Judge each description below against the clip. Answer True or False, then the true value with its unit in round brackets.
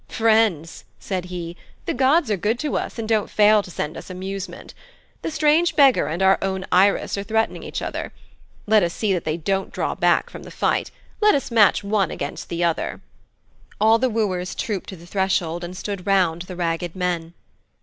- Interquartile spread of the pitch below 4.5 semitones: True (3.8 semitones)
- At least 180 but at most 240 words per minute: True (195 wpm)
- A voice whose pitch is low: False (195 Hz)